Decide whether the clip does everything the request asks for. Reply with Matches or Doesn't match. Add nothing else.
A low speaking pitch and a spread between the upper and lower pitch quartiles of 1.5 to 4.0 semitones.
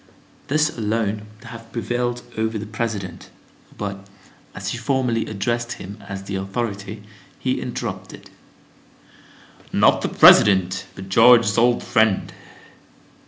Matches